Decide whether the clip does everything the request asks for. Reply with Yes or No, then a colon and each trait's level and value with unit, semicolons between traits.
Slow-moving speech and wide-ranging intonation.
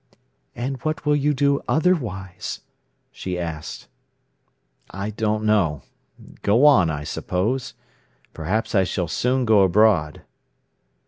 Yes: slow, 110 wpm; wide, 6.4 semitones